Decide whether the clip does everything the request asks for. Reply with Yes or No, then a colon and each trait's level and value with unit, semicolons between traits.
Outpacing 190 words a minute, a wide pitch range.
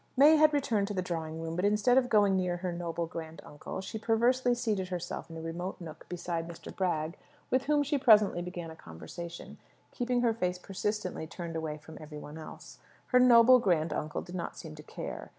Yes: fast, 205 wpm; wide, 5.7 semitones